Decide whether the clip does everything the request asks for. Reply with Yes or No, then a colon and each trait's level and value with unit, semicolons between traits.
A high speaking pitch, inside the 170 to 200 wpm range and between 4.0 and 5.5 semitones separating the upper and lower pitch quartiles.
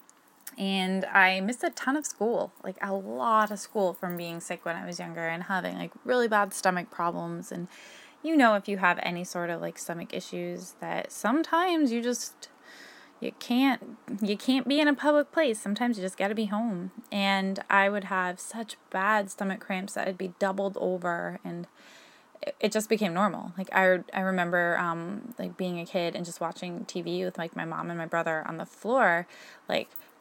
Yes: high, 195 Hz; average, 195 wpm; average, 4.4 semitones